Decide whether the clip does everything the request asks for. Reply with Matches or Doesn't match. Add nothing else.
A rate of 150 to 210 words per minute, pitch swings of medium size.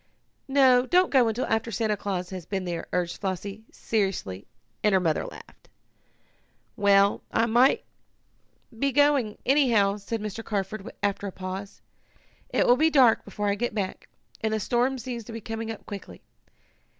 Matches